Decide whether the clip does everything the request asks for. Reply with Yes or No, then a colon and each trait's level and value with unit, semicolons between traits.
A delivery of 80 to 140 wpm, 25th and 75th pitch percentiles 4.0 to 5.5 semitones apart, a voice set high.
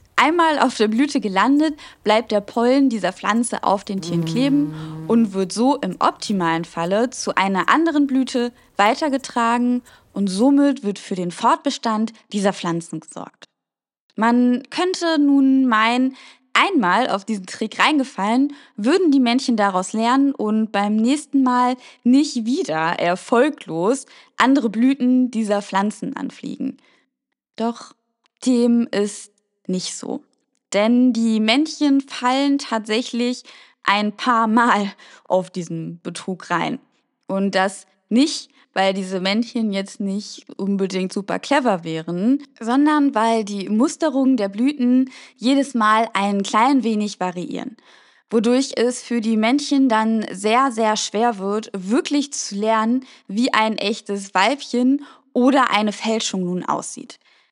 Yes: average, 130 wpm; average, 4.7 semitones; high, 230 Hz